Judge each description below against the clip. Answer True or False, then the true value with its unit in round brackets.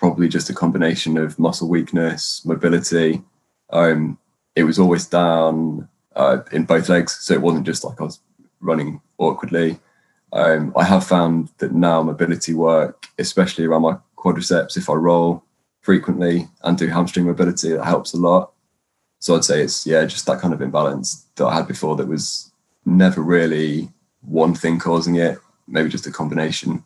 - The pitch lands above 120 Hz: False (85 Hz)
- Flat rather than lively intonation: True (1.2 semitones)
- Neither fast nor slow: True (170 wpm)